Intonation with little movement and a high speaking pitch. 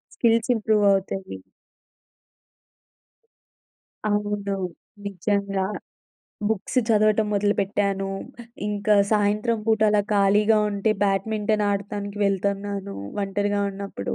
Yes: narrow, 1.2 semitones; high, 205 Hz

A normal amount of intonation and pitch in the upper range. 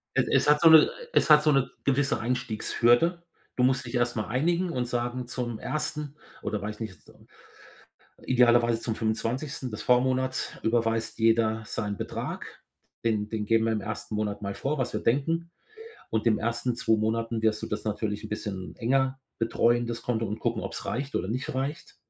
No: average, 3.0 semitones; low, 120 Hz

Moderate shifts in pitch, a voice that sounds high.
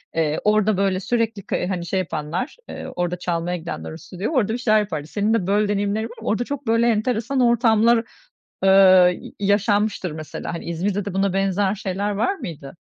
Yes: average, 3.6 semitones; high, 205 Hz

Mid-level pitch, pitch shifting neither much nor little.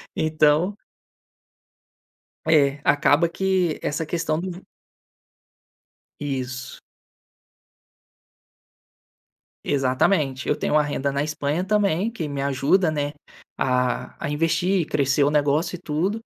Yes: medium, 150 Hz; average, 3.5 semitones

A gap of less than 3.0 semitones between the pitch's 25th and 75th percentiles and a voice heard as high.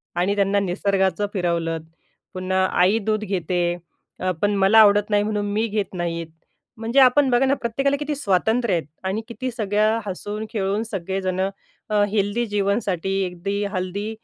Yes: narrow, 2.6 semitones; high, 205 Hz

